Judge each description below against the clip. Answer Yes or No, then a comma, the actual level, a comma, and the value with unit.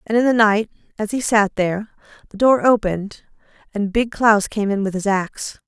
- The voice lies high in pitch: Yes, high, 210 Hz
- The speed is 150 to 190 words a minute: No, average, 200 wpm